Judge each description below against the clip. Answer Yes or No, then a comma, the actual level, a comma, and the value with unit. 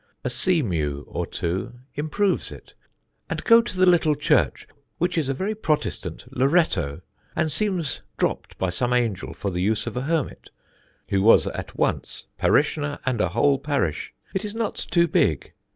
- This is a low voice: No, medium, 145 Hz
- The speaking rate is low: No, average, 170 wpm